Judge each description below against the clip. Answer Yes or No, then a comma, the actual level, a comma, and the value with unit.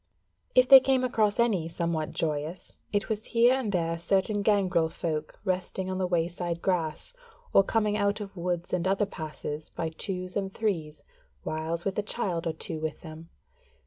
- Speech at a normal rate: Yes, average, 175 wpm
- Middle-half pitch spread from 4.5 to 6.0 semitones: No, average, 3.8 semitones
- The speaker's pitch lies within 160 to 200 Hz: Yes, medium, 185 Hz